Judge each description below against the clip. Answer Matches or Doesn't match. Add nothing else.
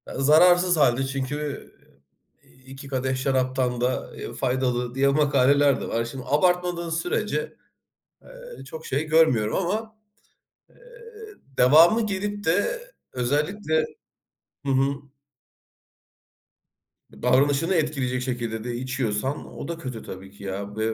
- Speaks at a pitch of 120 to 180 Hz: Matches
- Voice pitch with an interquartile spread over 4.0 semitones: Matches